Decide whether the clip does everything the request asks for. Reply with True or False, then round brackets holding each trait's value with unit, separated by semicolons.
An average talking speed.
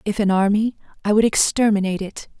True (175 wpm)